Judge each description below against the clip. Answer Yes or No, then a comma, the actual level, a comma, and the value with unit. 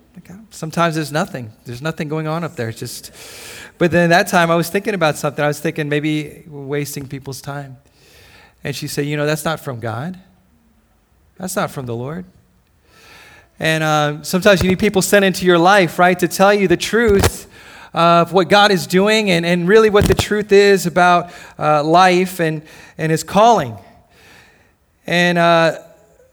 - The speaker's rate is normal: Yes, average, 180 wpm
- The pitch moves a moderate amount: Yes, average, 3.9 semitones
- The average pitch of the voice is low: No, medium, 170 Hz